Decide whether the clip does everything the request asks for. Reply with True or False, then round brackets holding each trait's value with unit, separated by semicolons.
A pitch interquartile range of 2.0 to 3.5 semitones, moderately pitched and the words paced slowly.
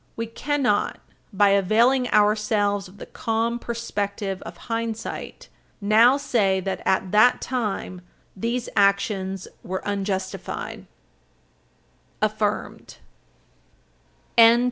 False (2.8 semitones; 210 Hz; 85 wpm)